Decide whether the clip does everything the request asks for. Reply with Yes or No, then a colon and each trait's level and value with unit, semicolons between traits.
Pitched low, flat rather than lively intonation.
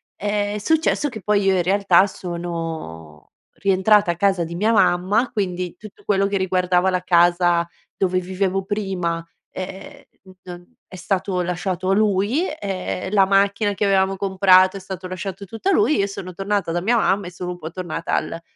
No: high, 190 Hz; narrow, 2.1 semitones